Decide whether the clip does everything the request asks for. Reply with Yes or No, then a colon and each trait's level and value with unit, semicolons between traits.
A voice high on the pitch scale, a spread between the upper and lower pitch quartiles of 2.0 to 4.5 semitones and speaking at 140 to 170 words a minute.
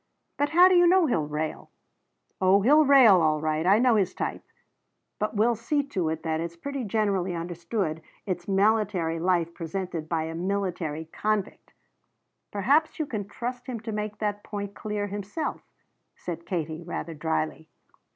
No: high, 195 Hz; average, 5.0 semitones; average, 165 wpm